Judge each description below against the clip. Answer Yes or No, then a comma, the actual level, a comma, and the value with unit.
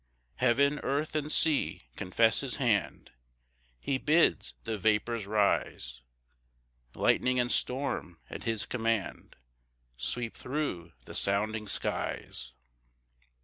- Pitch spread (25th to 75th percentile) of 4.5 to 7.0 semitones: Yes, average, 5.2 semitones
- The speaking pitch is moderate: No, low, 115 Hz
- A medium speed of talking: No, slow, 105 wpm